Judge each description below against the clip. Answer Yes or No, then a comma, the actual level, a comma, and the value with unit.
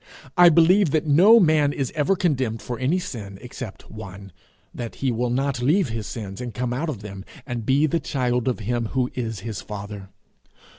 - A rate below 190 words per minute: No, average, 195 wpm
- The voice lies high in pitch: No, low, 125 Hz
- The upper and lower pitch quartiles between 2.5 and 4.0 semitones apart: No, average, 5.0 semitones